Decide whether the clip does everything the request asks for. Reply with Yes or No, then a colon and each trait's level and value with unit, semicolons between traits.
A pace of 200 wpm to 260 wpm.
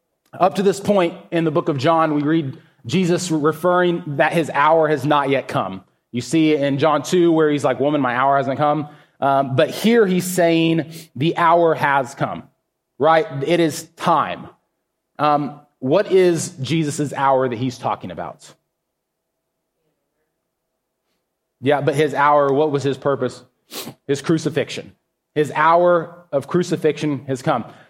No: average, 155 wpm